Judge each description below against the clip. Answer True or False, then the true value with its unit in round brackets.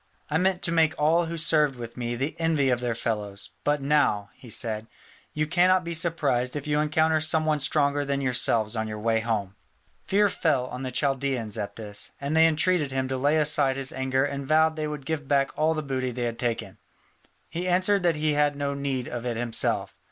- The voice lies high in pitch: False (140 Hz)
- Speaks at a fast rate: True (215 wpm)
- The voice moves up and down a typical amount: True (4.2 semitones)